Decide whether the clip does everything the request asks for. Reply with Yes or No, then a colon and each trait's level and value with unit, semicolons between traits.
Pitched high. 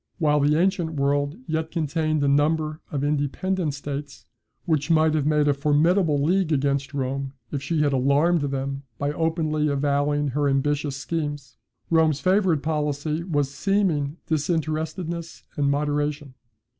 No: medium, 150 Hz